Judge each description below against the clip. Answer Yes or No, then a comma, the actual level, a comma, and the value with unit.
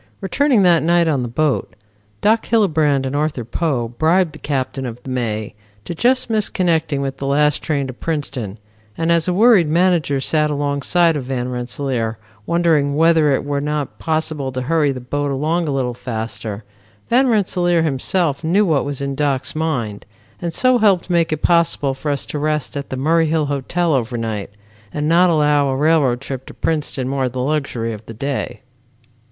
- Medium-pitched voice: Yes, medium, 145 Hz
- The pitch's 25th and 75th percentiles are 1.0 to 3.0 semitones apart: No, average, 3.9 semitones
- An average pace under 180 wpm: No, average, 185 wpm